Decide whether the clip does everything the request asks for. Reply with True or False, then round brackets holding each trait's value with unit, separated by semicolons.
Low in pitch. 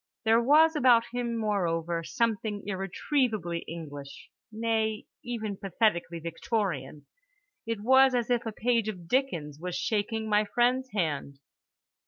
False (215 Hz)